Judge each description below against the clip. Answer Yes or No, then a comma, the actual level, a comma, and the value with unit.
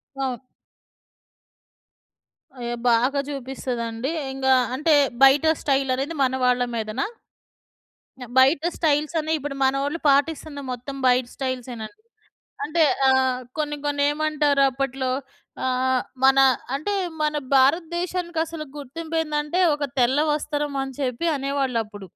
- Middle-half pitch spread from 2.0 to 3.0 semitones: Yes, average, 2.7 semitones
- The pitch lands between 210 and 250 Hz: No, very high, 275 Hz